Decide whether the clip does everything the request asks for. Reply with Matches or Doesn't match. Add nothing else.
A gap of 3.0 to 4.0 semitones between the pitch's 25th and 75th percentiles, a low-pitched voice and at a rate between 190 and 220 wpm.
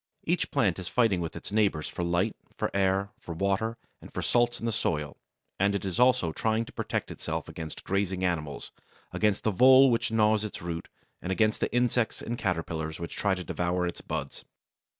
Doesn't match